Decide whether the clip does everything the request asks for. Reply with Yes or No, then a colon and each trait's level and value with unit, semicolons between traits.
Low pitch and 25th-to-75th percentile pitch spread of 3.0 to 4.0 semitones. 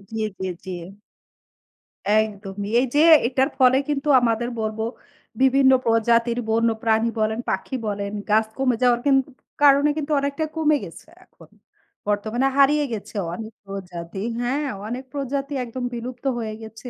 No: high, 235 Hz; average, 3.7 semitones